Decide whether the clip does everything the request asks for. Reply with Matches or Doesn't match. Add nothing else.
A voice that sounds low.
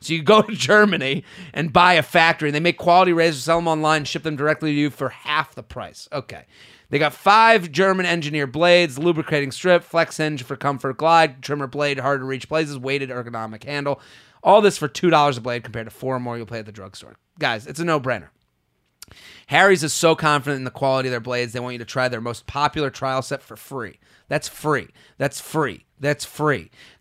Doesn't match